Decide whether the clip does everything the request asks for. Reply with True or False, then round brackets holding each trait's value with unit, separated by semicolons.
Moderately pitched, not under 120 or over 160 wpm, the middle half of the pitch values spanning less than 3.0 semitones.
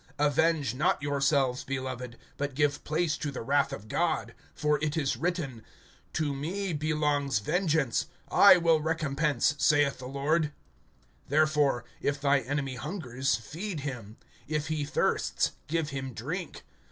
True (145 Hz; 140 wpm; 2.6 semitones)